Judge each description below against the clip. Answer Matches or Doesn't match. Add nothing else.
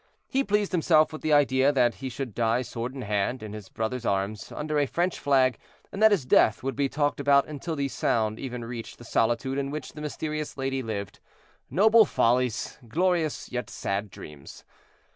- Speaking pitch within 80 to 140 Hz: Matches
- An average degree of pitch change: Matches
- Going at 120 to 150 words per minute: Doesn't match